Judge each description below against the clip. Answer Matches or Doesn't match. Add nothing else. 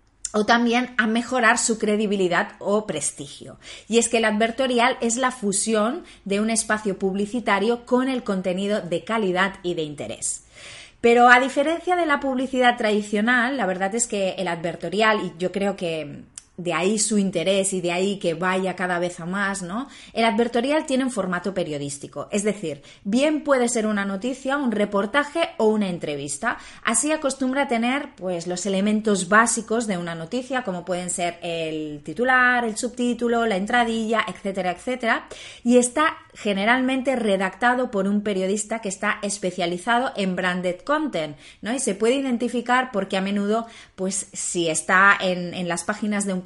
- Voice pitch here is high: Matches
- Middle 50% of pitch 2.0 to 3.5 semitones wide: Doesn't match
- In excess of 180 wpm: Doesn't match